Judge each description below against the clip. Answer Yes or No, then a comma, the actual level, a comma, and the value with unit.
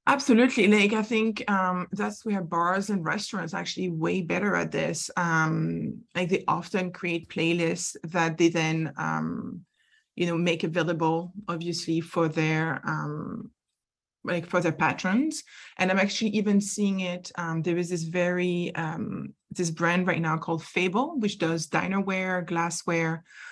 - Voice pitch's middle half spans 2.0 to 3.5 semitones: Yes, average, 3.2 semitones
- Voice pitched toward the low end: No, medium, 180 Hz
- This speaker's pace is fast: No, average, 155 wpm